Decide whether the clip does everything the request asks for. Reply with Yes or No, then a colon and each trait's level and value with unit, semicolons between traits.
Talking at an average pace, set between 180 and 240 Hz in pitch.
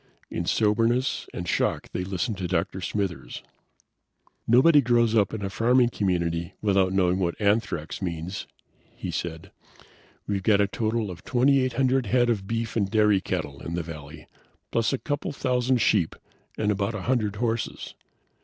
No: average, 165 wpm; low, 105 Hz